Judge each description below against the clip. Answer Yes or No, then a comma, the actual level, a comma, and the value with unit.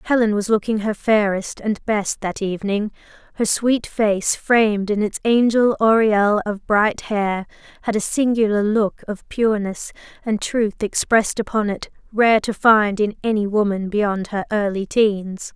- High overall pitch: Yes, high, 210 Hz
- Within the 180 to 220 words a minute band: No, average, 155 wpm